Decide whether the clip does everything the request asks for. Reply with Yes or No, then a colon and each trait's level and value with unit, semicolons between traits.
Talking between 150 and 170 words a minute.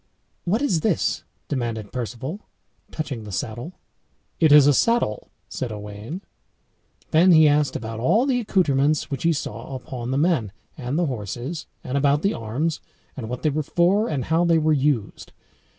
Yes: average, 165 wpm